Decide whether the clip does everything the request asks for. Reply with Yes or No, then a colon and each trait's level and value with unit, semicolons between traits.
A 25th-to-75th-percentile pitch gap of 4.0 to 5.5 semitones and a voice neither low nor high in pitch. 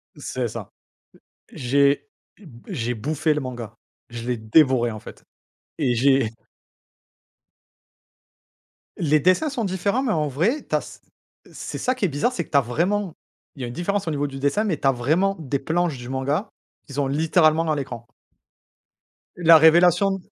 Yes: average, 5.2 semitones; medium, 150 Hz